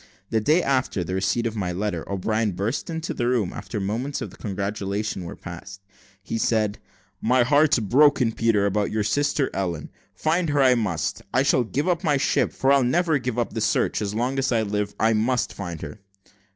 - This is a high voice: No, low, 110 Hz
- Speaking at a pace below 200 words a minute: No, fast, 205 wpm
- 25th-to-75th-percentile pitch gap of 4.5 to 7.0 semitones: Yes, average, 4.8 semitones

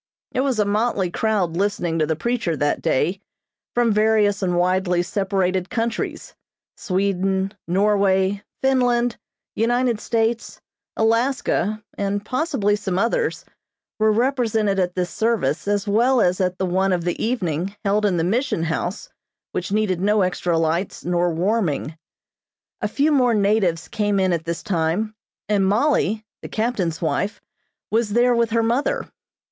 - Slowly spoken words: No, average, 145 wpm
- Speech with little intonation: No, average, 3.9 semitones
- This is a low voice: No, high, 205 Hz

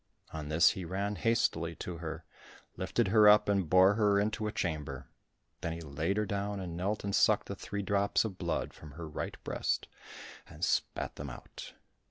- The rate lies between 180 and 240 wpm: Yes, average, 185 wpm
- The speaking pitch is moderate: No, very low, 95 Hz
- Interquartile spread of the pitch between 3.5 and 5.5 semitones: Yes, average, 3.9 semitones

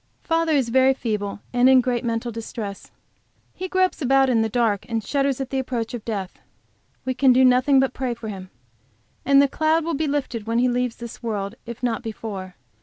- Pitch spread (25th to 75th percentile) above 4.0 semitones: No, average, 3.0 semitones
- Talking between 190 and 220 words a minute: Yes, fast, 205 wpm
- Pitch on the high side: Yes, high, 245 Hz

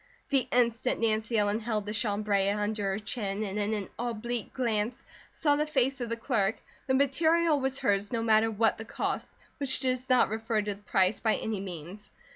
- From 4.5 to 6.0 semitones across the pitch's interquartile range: No, average, 3.4 semitones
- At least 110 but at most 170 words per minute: No, average, 195 wpm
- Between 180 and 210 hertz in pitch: No, high, 220 Hz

